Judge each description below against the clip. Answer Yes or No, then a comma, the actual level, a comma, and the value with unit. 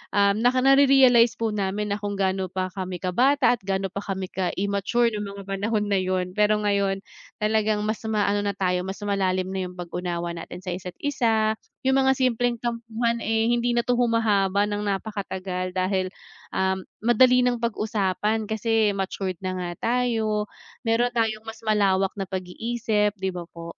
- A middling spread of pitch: Yes, average, 3.3 semitones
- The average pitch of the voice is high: Yes, high, 205 Hz